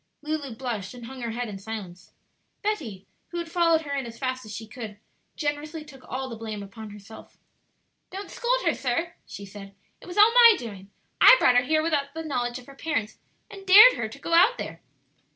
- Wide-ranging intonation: Yes, wide, 6.8 semitones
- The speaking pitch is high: Yes, very high, 260 Hz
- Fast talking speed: Yes, fast, 210 wpm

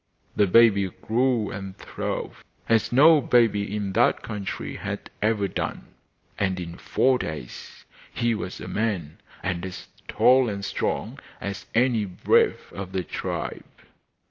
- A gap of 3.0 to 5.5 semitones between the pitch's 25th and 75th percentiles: Yes, average, 3.4 semitones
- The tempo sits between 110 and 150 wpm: Yes, average, 140 wpm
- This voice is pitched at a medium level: No, low, 105 Hz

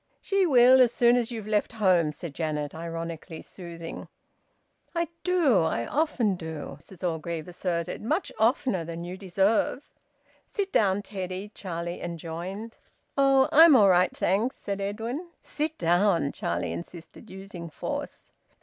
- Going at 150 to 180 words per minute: No, average, 140 wpm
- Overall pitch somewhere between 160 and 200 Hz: Yes, high, 190 Hz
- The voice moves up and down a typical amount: No, wide, 6.1 semitones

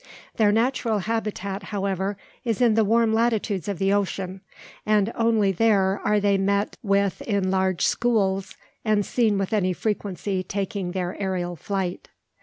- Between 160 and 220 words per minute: No, average, 150 wpm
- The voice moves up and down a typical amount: No, narrow, 2.3 semitones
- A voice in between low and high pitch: No, high, 200 Hz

